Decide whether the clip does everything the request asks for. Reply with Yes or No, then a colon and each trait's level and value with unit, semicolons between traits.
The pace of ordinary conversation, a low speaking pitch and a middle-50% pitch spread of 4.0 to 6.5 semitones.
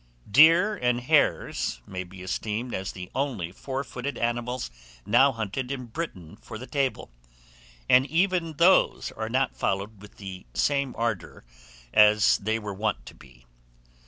Yes: average, 150 wpm; low, 115 Hz; wide, 5.6 semitones